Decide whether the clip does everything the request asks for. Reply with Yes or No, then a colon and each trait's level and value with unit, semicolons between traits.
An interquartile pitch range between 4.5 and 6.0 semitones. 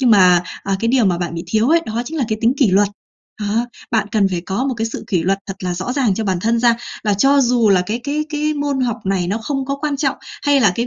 Yes: wide, 5.5 semitones